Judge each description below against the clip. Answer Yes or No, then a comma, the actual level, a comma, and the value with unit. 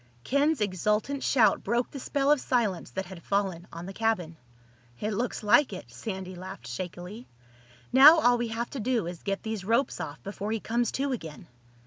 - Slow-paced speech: No, average, 185 wpm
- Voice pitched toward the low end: No, high, 210 Hz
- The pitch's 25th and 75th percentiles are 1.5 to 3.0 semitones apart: No, average, 4.8 semitones